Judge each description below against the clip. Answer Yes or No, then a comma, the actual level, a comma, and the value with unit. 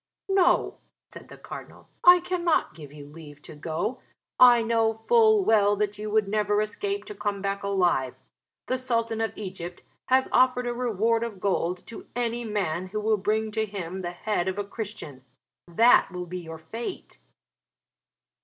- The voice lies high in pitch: Yes, high, 210 Hz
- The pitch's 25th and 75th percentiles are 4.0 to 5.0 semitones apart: Yes, average, 4.3 semitones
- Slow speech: No, average, 170 wpm